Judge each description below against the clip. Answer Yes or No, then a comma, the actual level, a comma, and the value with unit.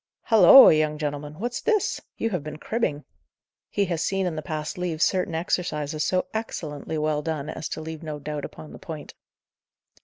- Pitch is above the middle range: No, medium, 155 Hz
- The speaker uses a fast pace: No, average, 180 wpm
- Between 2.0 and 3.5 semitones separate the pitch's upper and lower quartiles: Yes, average, 3.2 semitones